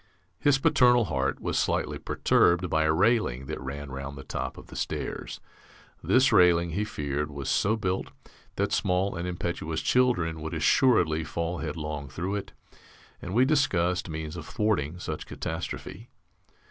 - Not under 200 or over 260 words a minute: No, average, 155 wpm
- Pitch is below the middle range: Yes, very low, 85 Hz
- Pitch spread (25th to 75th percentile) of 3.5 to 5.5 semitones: Yes, average, 5.1 semitones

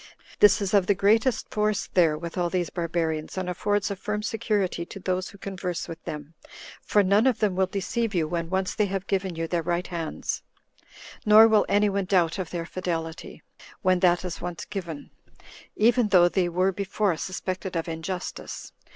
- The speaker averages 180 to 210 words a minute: Yes, average, 185 wpm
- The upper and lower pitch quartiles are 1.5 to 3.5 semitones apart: Yes, average, 2.8 semitones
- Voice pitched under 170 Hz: No, medium, 185 Hz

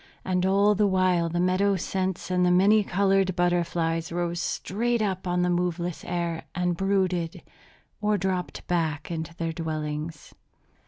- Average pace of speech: Yes, average, 150 wpm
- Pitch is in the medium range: Yes, medium, 180 Hz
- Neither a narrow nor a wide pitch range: No, narrow, 2.1 semitones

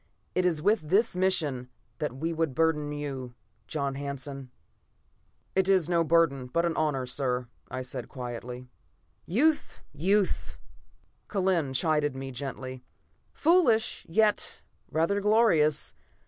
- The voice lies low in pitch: No, medium, 150 Hz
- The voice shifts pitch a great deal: Yes, wide, 5.7 semitones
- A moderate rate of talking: No, slow, 120 wpm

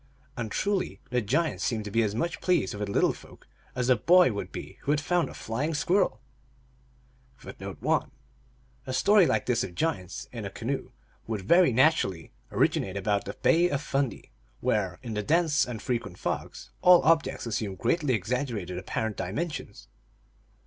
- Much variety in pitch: Yes, wide, 7.4 semitones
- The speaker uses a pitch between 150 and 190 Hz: No, low, 125 Hz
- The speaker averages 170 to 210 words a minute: Yes, average, 175 wpm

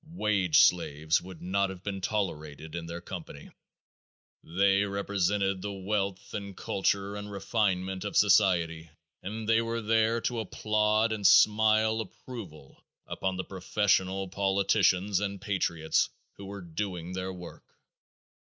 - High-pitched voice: No, low, 100 Hz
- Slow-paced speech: Yes, slow, 130 wpm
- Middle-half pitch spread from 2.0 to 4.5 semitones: Yes, narrow, 2.5 semitones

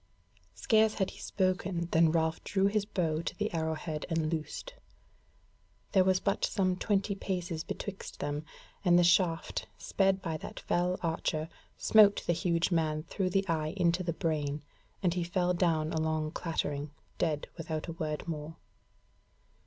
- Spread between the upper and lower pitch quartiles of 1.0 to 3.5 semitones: Yes, average, 2.9 semitones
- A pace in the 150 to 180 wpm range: Yes, average, 160 wpm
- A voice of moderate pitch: Yes, medium, 170 Hz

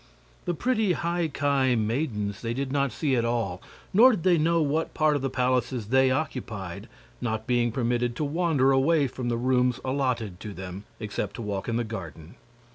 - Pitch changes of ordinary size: Yes, average, 4.3 semitones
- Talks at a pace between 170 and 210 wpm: Yes, average, 190 wpm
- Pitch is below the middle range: Yes, low, 125 Hz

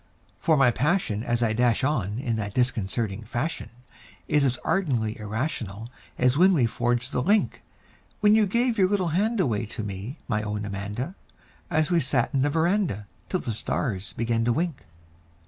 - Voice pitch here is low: Yes, low, 125 Hz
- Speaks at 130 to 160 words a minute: No, average, 175 wpm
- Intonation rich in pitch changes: Yes, wide, 7.0 semitones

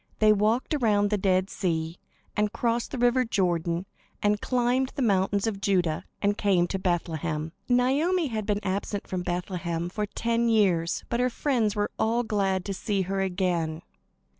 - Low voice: No, high, 200 Hz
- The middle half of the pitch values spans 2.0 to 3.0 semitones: No, average, 4.3 semitones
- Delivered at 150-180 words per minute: Yes, average, 165 wpm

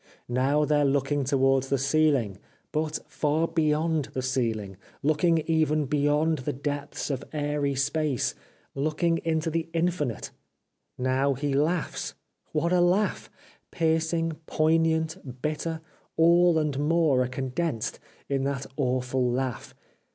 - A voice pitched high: No, medium, 150 Hz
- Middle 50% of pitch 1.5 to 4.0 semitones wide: Yes, average, 3.1 semitones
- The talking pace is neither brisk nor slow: No, slow, 130 wpm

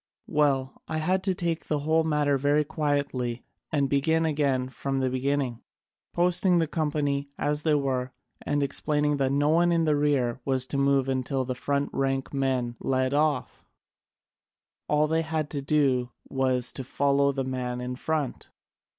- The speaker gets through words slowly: No, average, 165 wpm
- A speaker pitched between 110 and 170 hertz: Yes, medium, 140 Hz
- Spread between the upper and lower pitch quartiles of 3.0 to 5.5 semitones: No, narrow, 2.5 semitones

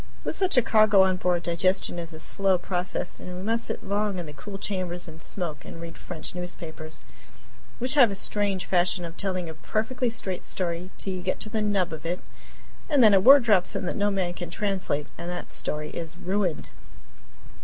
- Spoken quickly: Yes, fast, 210 wpm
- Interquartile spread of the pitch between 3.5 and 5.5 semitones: No, average, 3.1 semitones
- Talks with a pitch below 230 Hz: Yes, medium, 185 Hz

